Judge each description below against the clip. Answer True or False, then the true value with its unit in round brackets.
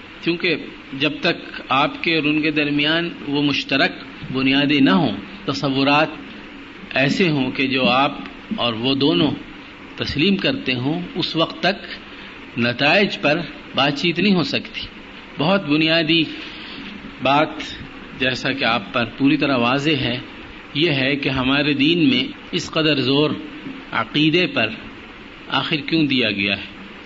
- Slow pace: False (140 wpm)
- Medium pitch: True (145 Hz)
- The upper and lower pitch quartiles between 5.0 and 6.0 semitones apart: False (3.2 semitones)